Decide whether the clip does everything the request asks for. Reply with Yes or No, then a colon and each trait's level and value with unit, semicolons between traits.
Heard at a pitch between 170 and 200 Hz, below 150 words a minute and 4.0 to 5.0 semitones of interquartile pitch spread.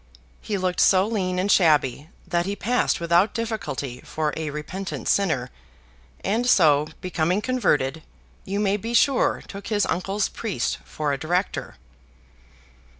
Yes: medium, 185 Hz; average, 140 wpm; average, 4.7 semitones